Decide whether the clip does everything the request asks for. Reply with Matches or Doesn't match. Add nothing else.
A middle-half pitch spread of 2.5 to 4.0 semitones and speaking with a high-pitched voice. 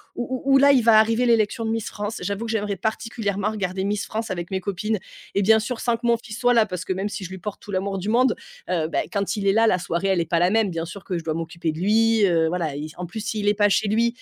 Matches